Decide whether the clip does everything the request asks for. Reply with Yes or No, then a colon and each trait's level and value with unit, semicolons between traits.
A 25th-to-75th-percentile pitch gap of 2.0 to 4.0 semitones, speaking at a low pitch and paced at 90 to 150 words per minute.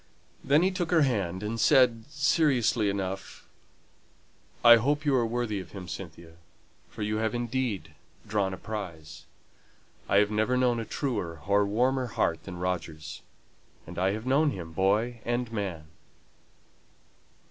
No: average, 5.0 semitones; low, 110 Hz; average, 145 wpm